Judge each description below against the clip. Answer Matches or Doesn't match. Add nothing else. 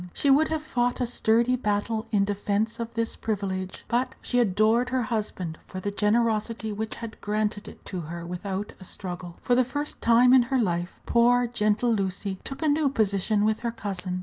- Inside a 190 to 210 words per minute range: Matches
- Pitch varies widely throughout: Doesn't match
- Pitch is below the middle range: Doesn't match